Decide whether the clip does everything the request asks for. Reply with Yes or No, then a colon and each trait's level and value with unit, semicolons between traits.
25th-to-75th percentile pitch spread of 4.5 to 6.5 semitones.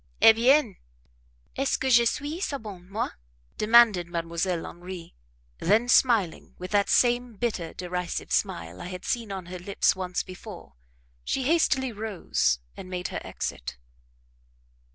Yes: average, 5.0 semitones